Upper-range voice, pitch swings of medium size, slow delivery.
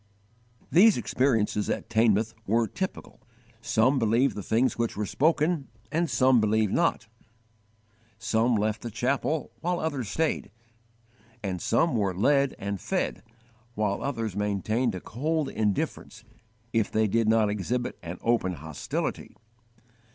No: low, 115 Hz; average, 4.6 semitones; slow, 130 wpm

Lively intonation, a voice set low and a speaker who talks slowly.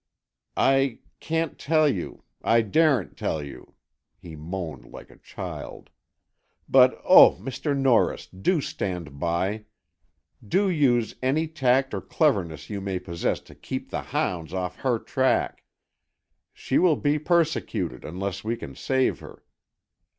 Yes: wide, 8.0 semitones; low, 115 Hz; slow, 130 wpm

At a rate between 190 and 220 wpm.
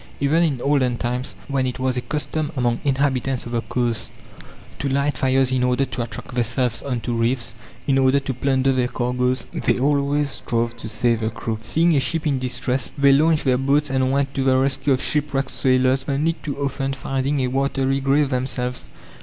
Yes: average, 195 wpm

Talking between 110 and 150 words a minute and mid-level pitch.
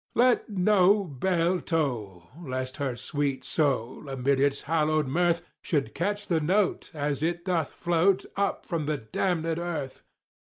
Yes: slow, 135 wpm; medium, 160 Hz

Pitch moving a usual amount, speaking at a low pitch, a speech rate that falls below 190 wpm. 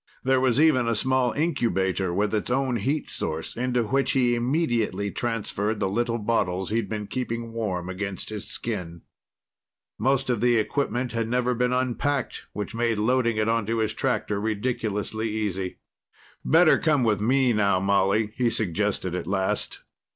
Yes: average, 3.5 semitones; low, 115 Hz; average, 160 wpm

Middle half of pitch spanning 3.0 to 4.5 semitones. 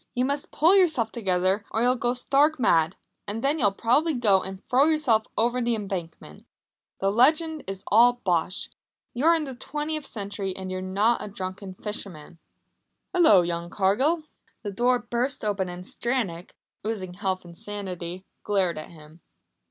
No: average, 5.2 semitones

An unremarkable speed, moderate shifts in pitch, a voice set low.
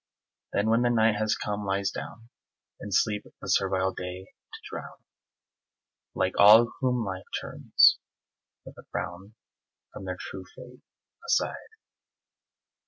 No: slow, 130 wpm; average, 3.1 semitones; low, 105 Hz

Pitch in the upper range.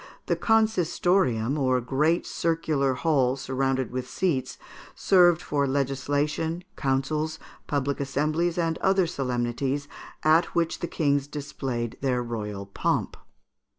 No: medium, 140 Hz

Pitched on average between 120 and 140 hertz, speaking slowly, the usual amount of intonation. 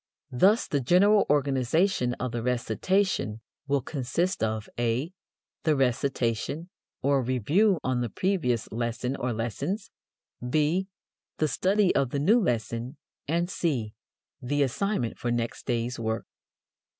No: low, 135 Hz; slow, 125 wpm; wide, 6.4 semitones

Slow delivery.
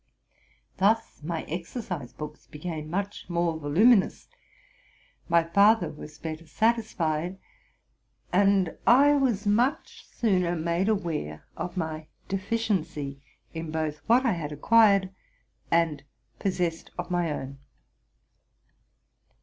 Yes: slow, 110 wpm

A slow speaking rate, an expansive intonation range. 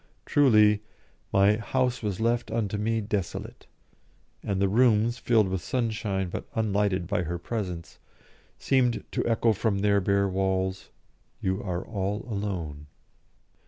No: slow, 130 wpm; average, 3.1 semitones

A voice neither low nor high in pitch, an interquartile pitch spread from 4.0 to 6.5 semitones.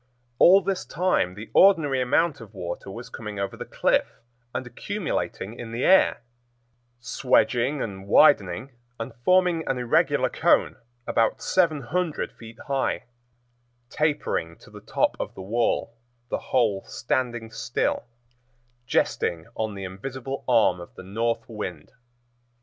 No: low, 120 Hz; wide, 5.5 semitones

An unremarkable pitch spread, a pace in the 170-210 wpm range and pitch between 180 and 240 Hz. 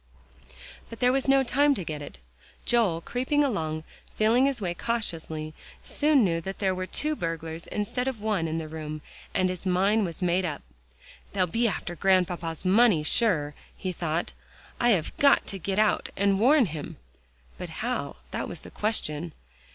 No: wide, 6.1 semitones; average, 175 wpm; high, 190 Hz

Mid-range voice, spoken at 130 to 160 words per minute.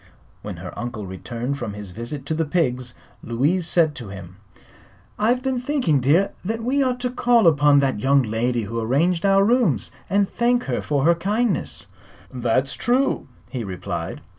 No: medium, 150 Hz; average, 170 wpm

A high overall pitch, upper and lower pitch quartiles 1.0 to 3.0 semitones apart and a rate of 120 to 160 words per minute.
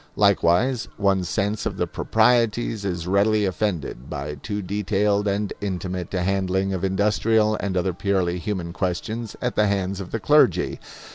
No: low, 100 Hz; narrow, 2.4 semitones; average, 155 wpm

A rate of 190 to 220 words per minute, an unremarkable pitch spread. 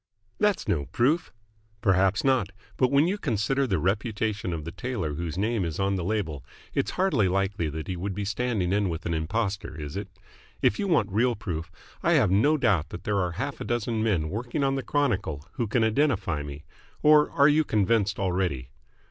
No: average, 200 wpm; wide, 5.9 semitones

